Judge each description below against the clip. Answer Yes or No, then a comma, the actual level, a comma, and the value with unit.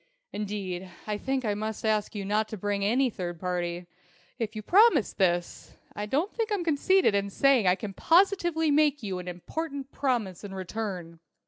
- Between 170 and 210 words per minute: Yes, average, 185 wpm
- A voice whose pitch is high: Yes, high, 215 Hz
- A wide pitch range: Yes, wide, 6.8 semitones